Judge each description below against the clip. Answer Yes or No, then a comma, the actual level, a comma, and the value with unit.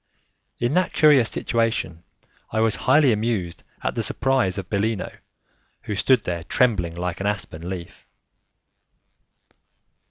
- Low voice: Yes, low, 105 Hz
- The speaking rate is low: Yes, slow, 125 wpm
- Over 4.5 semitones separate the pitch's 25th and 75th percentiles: Yes, average, 5.1 semitones